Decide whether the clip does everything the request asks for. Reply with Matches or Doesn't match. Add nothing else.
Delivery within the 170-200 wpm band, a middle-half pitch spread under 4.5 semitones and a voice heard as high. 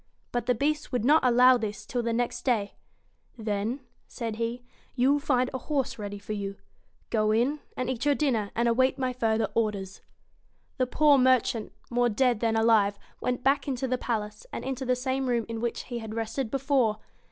Matches